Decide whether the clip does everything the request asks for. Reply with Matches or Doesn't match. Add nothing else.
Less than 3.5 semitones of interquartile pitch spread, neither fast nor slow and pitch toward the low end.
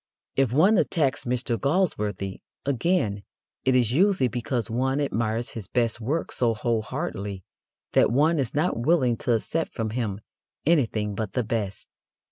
Doesn't match